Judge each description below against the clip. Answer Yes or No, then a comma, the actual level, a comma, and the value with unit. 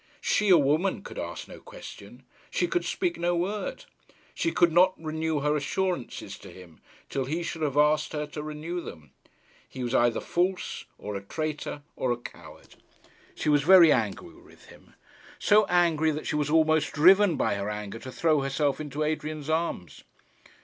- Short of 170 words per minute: No, average, 175 wpm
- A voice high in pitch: No, medium, 155 Hz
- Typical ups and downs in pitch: Yes, average, 3.9 semitones